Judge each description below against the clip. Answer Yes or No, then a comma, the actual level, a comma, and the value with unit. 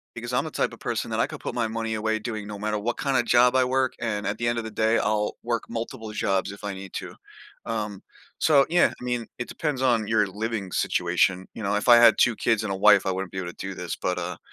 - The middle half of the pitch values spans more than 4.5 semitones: No, average, 2.9 semitones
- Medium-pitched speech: No, low, 110 Hz